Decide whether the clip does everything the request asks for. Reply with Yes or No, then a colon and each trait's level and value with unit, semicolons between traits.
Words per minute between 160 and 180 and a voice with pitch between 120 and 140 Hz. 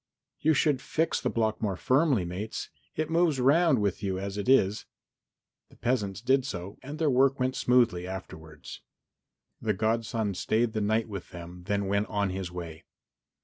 No: average, 170 wpm; low, 110 Hz